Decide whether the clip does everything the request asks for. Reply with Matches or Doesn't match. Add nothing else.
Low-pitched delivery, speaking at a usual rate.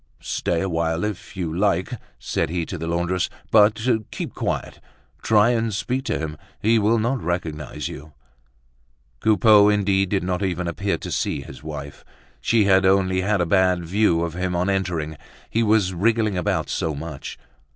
Matches